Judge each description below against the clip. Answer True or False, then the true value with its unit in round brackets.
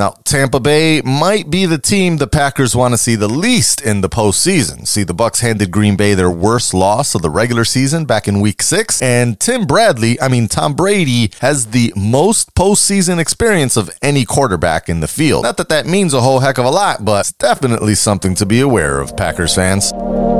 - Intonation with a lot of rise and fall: True (5.7 semitones)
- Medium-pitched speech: False (120 Hz)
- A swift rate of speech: True (210 wpm)